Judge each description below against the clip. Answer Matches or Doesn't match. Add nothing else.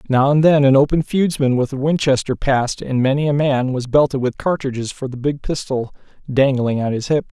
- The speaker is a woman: Doesn't match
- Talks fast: Matches